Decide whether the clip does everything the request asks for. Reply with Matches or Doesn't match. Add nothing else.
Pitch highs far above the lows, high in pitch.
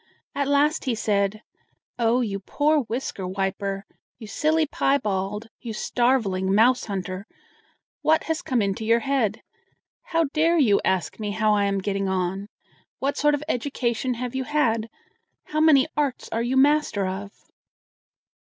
Matches